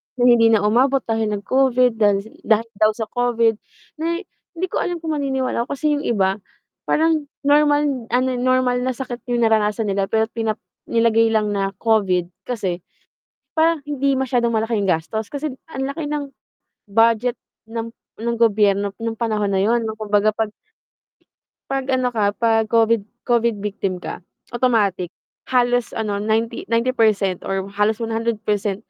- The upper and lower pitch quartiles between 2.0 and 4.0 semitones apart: Yes, average, 3.3 semitones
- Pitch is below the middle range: No, high, 230 Hz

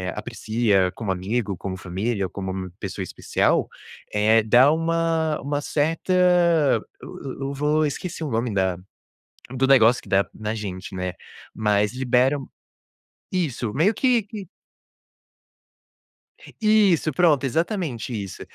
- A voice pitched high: No, low, 120 Hz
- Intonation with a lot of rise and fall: Yes, wide, 7.3 semitones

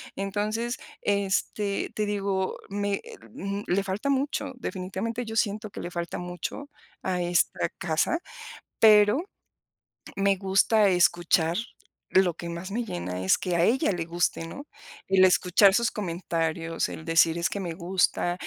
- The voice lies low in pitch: No, high, 190 Hz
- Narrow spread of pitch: No, average, 3.2 semitones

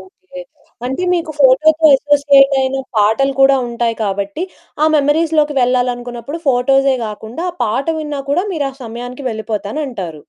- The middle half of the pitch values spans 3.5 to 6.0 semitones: Yes, average, 3.9 semitones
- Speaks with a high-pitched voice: Yes, very high, 270 Hz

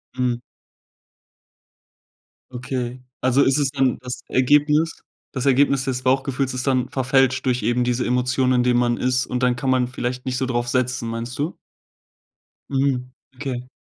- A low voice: Yes, low, 125 Hz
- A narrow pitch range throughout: Yes, narrow, 1.2 semitones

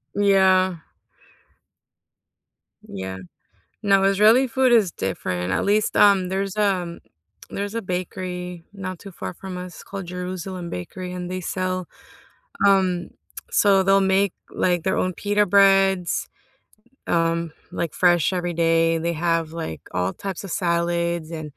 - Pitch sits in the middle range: Yes, medium, 180 Hz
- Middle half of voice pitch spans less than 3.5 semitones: Yes, narrow, 2.4 semitones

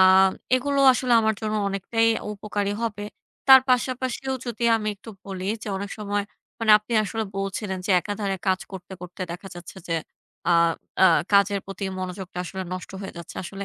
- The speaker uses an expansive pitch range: No, average, 2.8 semitones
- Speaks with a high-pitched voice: Yes, high, 200 Hz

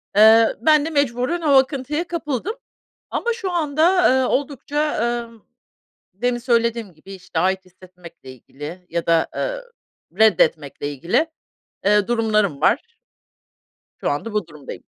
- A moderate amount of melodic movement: No, wide, 8.4 semitones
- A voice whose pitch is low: No, high, 230 Hz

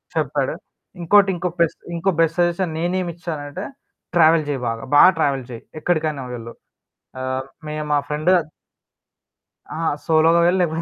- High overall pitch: No, medium, 160 Hz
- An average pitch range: Yes, average, 3.1 semitones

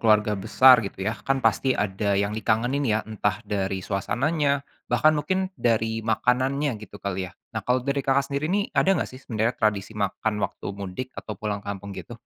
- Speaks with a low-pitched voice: Yes, low, 110 Hz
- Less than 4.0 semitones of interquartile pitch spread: No, average, 4.7 semitones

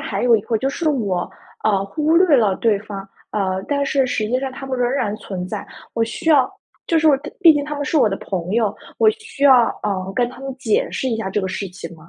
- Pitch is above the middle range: Yes, high, 235 Hz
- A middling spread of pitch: No, wide, 6.0 semitones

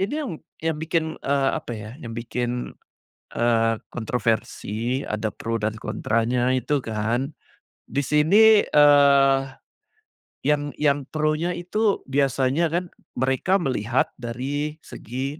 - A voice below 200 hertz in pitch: Yes, low, 135 Hz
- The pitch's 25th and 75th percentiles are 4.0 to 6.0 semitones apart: Yes, average, 4.3 semitones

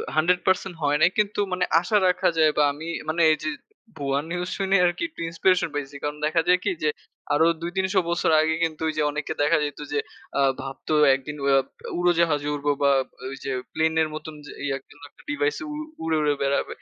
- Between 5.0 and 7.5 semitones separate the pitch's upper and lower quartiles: No, average, 3.4 semitones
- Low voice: No, medium, 160 Hz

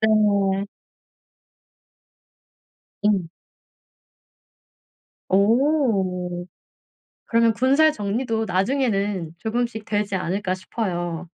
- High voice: Yes, high, 205 Hz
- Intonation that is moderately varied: Yes, average, 3.6 semitones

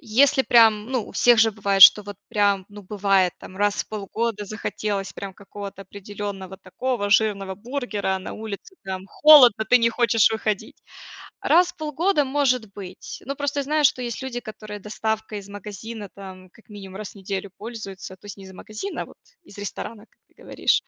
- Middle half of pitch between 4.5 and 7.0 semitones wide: No, average, 3.1 semitones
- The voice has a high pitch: Yes, high, 210 Hz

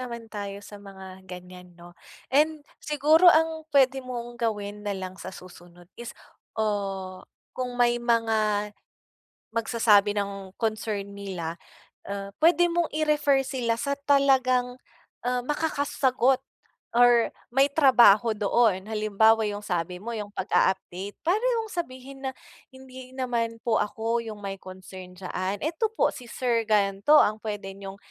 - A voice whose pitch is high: Yes, high, 225 Hz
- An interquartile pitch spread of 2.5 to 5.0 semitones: Yes, average, 4.6 semitones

